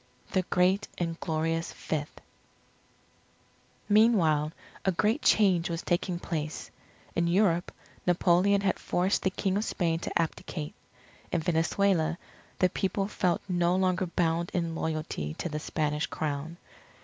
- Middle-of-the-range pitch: Yes, medium, 175 Hz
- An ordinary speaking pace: No, slow, 130 wpm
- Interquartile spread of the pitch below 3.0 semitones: Yes, narrow, 2.5 semitones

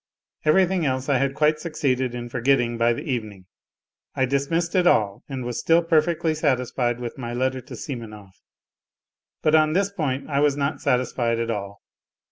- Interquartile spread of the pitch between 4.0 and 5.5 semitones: Yes, average, 4.4 semitones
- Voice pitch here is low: Yes, low, 130 Hz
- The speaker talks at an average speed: Yes, average, 175 wpm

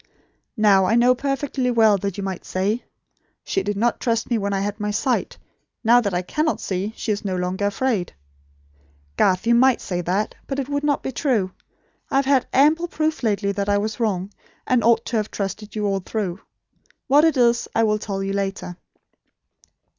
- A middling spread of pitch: Yes, average, 4.2 semitones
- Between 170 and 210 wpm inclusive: Yes, average, 200 wpm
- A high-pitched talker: Yes, high, 215 Hz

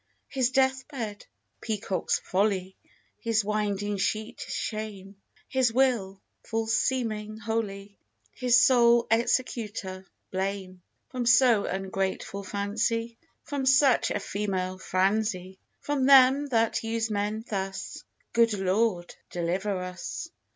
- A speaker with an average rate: No, slow, 110 wpm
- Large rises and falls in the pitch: No, average, 3.4 semitones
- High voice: Yes, high, 215 Hz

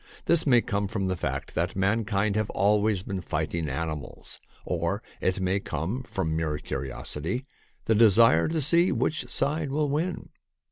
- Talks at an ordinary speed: Yes, average, 160 wpm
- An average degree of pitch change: No, wide, 6.7 semitones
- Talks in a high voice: No, low, 100 Hz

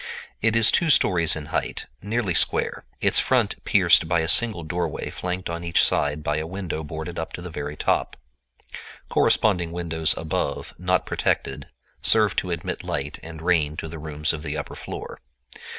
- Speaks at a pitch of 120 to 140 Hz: No, very low, 85 Hz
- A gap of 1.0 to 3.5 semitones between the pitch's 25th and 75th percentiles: Yes, narrow, 2.6 semitones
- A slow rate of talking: No, average, 175 wpm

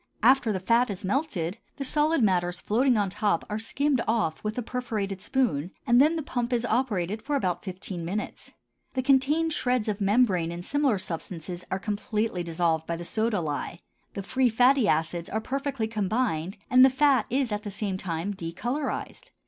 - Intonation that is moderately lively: No, wide, 5.9 semitones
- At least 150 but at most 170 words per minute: No, average, 180 wpm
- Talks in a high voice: Yes, high, 215 Hz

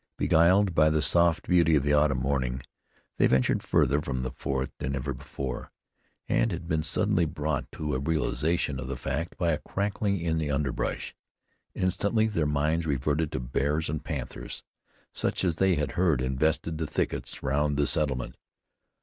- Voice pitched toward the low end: Yes, very low, 75 Hz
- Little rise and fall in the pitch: No, average, 3.4 semitones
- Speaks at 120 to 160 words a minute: No, average, 170 wpm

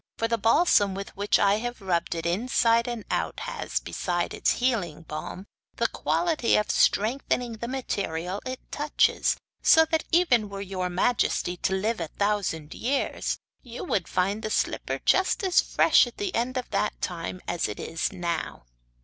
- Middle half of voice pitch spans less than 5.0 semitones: No, wide, 5.4 semitones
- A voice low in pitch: No, high, 210 Hz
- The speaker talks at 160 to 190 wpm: Yes, average, 170 wpm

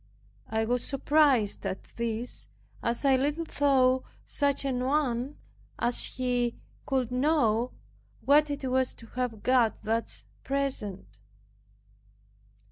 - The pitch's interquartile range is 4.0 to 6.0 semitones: No, average, 3.0 semitones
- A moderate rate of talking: No, slow, 115 wpm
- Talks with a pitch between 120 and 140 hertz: No, very high, 255 Hz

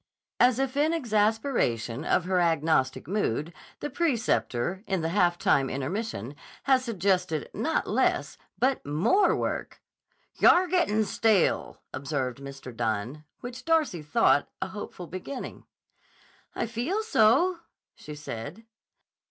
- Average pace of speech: No, slow, 120 wpm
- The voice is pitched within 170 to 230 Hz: Yes, high, 190 Hz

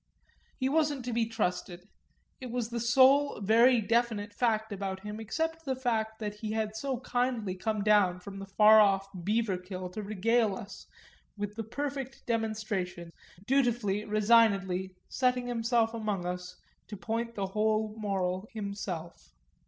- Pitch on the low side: No, high, 215 Hz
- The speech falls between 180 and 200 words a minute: No, average, 145 wpm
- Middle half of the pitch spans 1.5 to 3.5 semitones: Yes, average, 3.2 semitones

